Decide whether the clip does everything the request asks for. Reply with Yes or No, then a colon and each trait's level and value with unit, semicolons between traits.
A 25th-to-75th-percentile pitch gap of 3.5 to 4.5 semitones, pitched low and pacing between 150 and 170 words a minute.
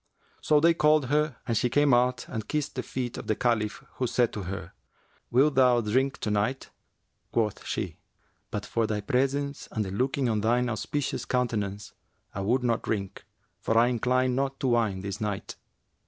No: average, 3.8 semitones; low, 120 Hz; average, 185 wpm